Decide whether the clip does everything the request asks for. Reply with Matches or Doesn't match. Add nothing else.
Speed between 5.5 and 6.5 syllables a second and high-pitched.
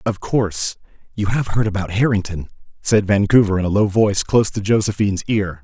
Doesn't match